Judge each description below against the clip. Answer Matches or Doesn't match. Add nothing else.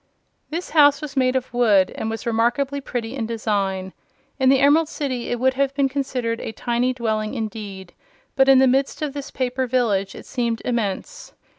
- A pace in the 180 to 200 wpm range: Matches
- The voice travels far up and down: Doesn't match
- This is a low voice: Doesn't match